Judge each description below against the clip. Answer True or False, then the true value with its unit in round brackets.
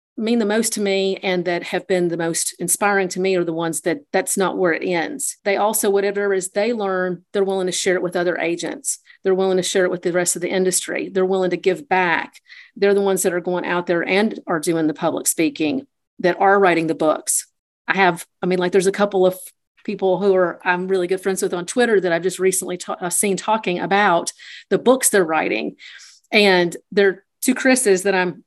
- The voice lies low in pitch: False (185 Hz)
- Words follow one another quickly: True (230 wpm)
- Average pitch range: False (2.1 semitones)